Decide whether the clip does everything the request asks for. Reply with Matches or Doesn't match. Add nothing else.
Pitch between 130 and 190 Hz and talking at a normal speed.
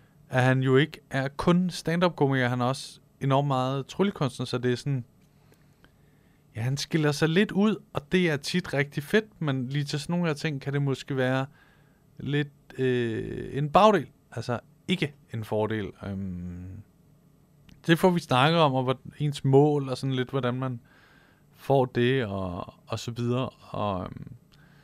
Matches